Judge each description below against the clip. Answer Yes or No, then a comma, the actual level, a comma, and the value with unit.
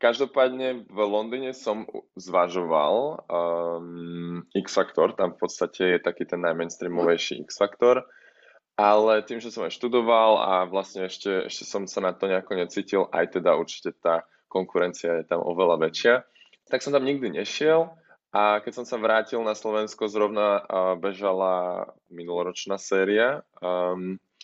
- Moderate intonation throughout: Yes, average, 3.9 semitones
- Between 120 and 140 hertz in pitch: No, low, 100 Hz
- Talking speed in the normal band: Yes, average, 145 wpm